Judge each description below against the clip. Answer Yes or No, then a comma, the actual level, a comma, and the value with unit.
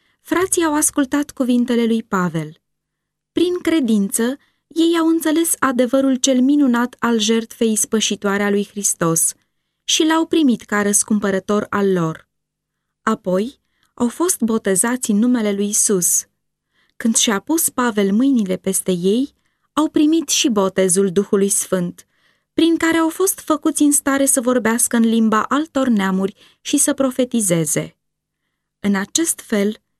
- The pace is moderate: Yes, average, 135 wpm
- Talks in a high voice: Yes, high, 235 Hz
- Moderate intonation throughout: No, wide, 6.2 semitones